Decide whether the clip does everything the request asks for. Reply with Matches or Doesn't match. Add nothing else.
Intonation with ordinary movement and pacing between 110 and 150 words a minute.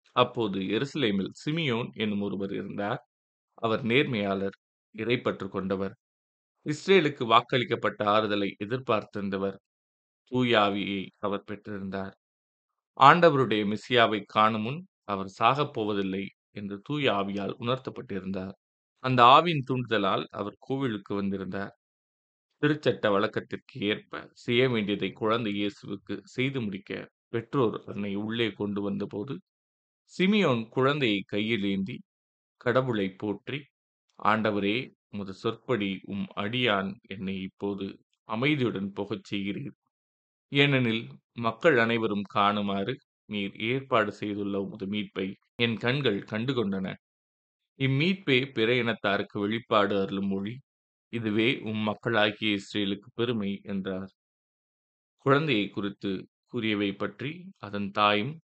Doesn't match